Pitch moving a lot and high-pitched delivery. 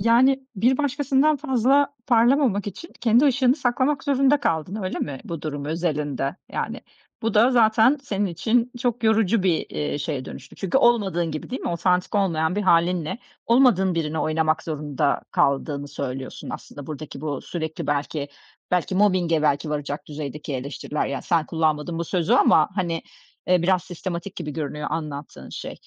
No: wide, 7.2 semitones; medium, 175 Hz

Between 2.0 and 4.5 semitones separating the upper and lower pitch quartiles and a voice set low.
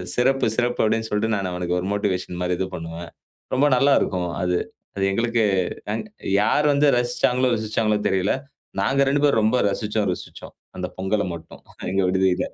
No: average, 4.9 semitones; low, 105 Hz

